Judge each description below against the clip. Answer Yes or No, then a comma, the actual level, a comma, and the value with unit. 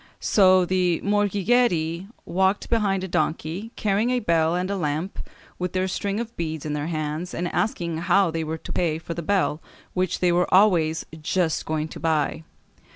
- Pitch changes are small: No, average, 3.4 semitones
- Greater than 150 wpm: Yes, average, 180 wpm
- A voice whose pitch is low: No, medium, 175 Hz